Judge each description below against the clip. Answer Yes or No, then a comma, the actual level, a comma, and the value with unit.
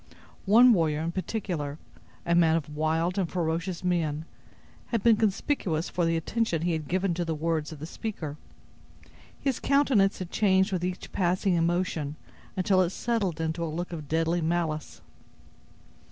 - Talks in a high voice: No, medium, 170 Hz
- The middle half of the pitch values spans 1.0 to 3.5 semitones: Yes, average, 3.0 semitones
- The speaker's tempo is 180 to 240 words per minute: No, average, 160 wpm